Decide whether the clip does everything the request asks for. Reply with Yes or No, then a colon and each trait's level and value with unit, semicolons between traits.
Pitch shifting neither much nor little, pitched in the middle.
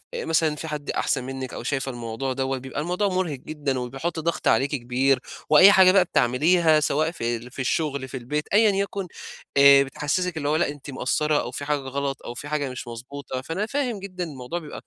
Yes: average, 4.0 semitones; medium, 145 Hz